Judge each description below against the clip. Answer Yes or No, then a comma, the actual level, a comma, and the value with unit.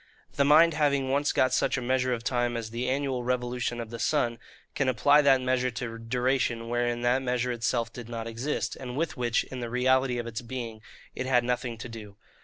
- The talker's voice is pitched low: Yes, low, 125 Hz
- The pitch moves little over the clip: Yes, narrow, 1.8 semitones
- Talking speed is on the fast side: Yes, fast, 210 wpm